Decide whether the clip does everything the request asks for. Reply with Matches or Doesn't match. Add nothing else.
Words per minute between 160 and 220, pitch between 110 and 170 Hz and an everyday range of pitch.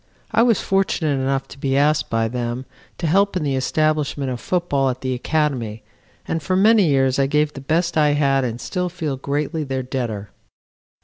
Matches